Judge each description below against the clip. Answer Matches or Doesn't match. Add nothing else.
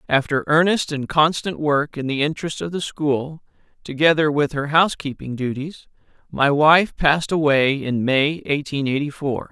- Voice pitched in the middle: Matches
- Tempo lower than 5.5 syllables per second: Matches